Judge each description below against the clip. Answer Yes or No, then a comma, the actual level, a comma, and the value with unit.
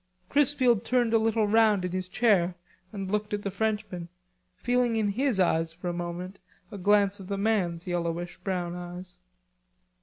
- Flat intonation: No, average, 3.7 semitones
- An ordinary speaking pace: Yes, average, 170 wpm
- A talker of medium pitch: No, high, 195 Hz